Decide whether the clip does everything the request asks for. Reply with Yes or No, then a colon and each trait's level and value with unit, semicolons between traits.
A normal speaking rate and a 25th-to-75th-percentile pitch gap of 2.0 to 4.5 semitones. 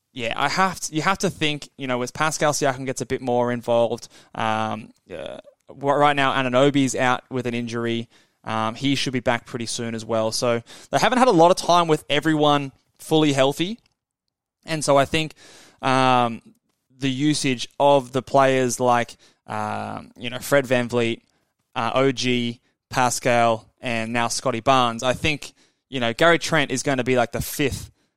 Yes: average, 180 wpm; average, 3.2 semitones